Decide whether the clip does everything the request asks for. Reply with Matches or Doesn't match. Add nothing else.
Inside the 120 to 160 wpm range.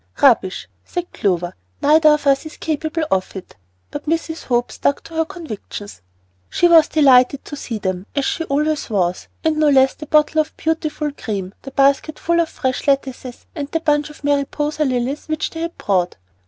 Doesn't match